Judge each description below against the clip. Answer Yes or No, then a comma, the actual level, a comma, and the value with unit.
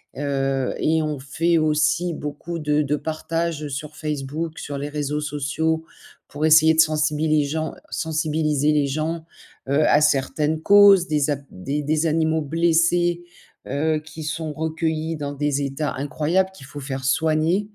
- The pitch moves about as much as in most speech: No, narrow, 1.6 semitones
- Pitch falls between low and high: Yes, medium, 155 Hz